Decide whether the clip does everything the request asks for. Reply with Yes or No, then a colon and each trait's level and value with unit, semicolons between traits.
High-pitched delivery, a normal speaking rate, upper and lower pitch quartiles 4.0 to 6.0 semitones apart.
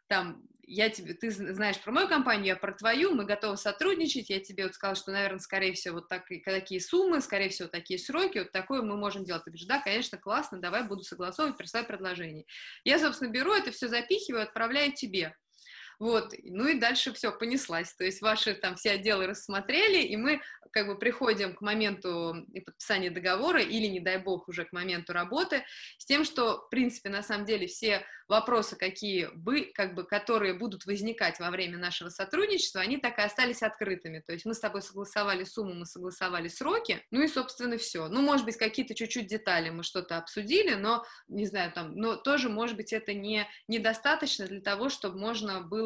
No: high, 210 Hz; fast, 195 wpm; average, 4.5 semitones